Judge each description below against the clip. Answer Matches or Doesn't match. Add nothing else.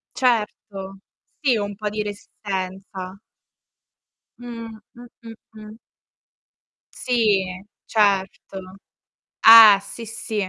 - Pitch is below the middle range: Doesn't match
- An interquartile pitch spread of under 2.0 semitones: Doesn't match